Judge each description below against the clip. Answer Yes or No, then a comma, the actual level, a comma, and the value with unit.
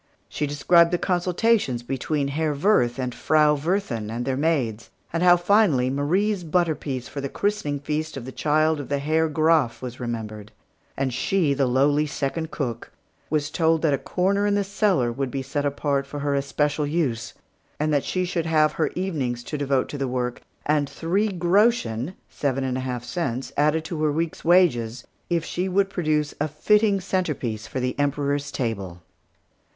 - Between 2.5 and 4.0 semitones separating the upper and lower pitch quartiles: No, average, 4.5 semitones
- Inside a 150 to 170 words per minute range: No, average, 185 wpm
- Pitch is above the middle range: No, medium, 150 Hz